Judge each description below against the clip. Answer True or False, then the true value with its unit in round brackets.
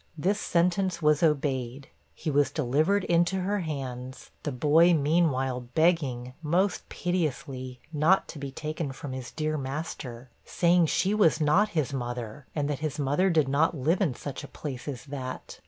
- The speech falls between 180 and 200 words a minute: False (165 wpm)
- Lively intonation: False (4.2 semitones)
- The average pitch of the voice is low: False (150 Hz)